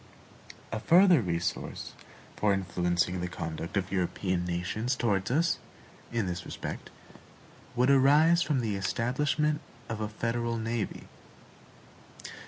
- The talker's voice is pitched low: Yes, low, 110 Hz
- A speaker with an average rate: No, slow, 115 wpm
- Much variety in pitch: Yes, wide, 6.2 semitones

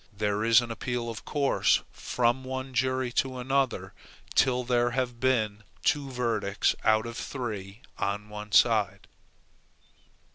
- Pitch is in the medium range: No, low, 120 Hz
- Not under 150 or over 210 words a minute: No, slow, 135 wpm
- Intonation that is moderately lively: Yes, average, 3.3 semitones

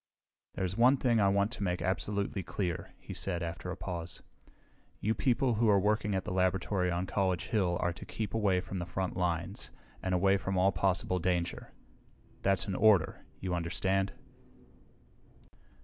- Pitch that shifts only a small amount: Yes, narrow, 2.2 semitones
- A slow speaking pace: No, average, 165 wpm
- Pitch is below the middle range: Yes, very low, 95 Hz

